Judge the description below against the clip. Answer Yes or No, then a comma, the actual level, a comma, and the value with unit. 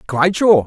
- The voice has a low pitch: No, medium, 170 Hz